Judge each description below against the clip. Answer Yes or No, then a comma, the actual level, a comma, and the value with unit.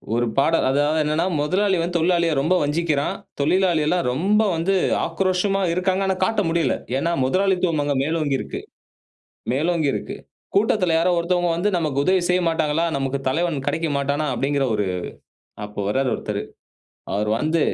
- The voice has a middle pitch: Yes, medium, 165 Hz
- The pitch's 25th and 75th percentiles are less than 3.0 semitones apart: No, average, 4.1 semitones